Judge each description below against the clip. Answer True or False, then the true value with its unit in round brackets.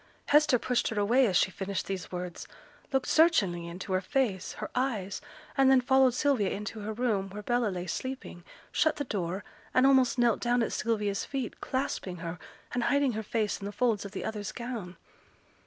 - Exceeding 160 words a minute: True (190 wpm)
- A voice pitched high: True (220 Hz)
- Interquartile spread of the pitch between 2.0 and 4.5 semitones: False (4.9 semitones)